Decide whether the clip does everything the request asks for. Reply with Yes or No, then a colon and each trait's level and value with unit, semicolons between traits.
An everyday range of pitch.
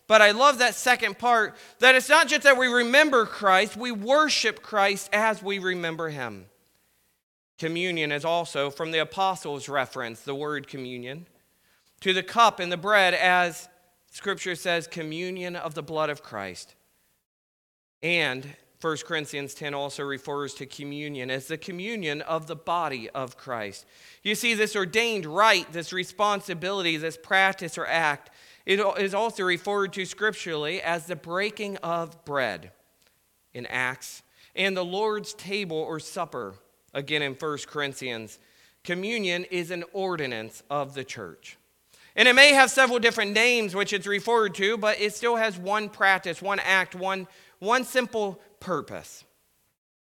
No: wide, 5.8 semitones